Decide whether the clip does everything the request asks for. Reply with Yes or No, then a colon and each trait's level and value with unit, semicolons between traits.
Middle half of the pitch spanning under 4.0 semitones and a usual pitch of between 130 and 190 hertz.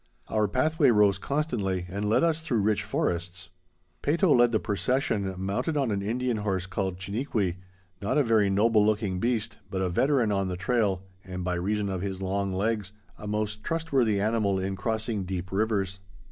No: average, 3.3 semitones; low, 105 Hz